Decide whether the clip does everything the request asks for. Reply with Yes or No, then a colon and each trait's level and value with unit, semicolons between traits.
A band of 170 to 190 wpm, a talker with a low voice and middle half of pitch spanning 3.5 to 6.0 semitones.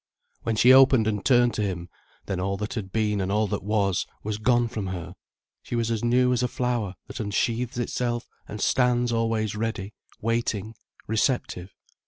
No: average, 180 wpm; low, 110 Hz; average, 2.8 semitones